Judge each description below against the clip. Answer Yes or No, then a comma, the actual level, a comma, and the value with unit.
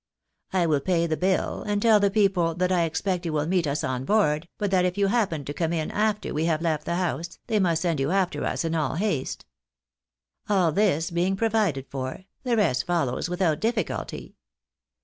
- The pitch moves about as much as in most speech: Yes, average, 3.9 semitones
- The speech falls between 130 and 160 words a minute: No, fast, 205 wpm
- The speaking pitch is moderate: Yes, medium, 175 Hz